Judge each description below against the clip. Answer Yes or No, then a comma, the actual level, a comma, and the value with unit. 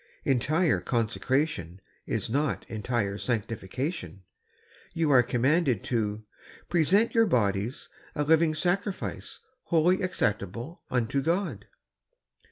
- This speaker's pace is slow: Yes, slow, 100 wpm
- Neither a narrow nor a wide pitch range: No, wide, 6.8 semitones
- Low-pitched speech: Yes, low, 130 Hz